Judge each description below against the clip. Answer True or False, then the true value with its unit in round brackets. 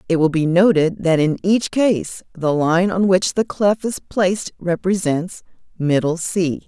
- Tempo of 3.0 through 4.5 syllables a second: True (4.1 syllables/s)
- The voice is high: False (180 Hz)